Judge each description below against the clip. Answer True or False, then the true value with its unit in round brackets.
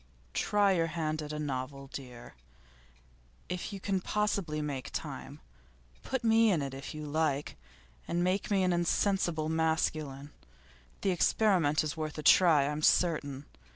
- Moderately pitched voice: True (160 Hz)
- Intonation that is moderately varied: True (4.0 semitones)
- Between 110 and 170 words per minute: True (150 wpm)